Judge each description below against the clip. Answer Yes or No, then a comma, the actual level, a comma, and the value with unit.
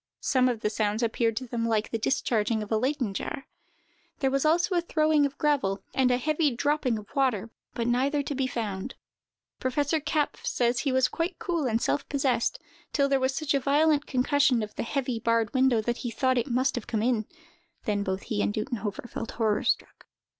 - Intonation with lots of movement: No, average, 3.9 semitones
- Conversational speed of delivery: No, fast, 210 wpm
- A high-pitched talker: Yes, very high, 255 Hz